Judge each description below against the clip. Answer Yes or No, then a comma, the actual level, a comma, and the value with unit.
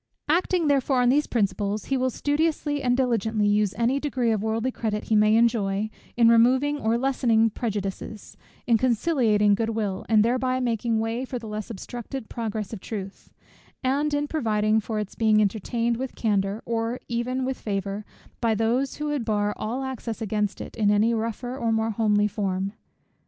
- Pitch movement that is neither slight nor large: Yes, average, 3.2 semitones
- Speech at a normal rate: Yes, average, 175 wpm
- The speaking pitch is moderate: No, high, 225 Hz